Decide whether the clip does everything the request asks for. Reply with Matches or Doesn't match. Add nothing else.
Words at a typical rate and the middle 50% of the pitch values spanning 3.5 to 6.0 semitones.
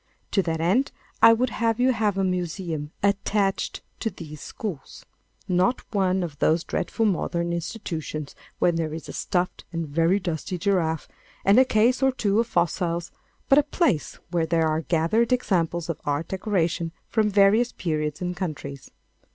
Matches